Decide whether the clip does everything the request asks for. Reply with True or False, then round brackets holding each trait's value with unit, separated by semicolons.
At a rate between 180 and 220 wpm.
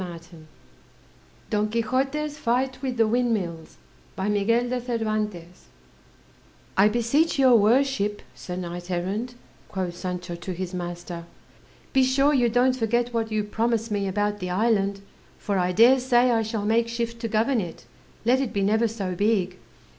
False (150 wpm)